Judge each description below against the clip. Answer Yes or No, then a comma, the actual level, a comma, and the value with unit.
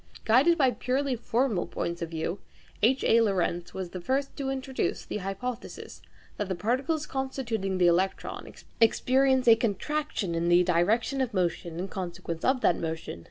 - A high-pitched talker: Yes, high, 215 Hz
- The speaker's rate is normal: Yes, average, 160 wpm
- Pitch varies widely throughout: Yes, wide, 6.8 semitones